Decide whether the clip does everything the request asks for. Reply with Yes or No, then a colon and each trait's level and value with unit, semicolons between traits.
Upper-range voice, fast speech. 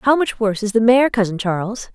Yes: high, 225 Hz; fast, 245 wpm